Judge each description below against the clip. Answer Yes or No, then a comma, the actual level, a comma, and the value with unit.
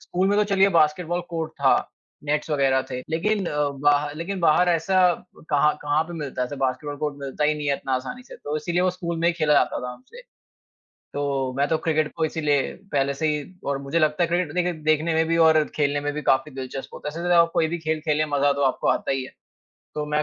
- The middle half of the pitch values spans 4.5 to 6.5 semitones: No, average, 2.8 semitones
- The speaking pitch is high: No, medium, 150 Hz